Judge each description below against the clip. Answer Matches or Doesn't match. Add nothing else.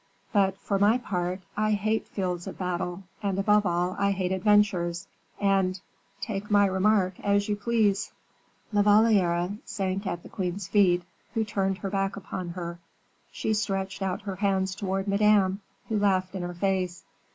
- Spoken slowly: Doesn't match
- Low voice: Doesn't match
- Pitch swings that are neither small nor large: Doesn't match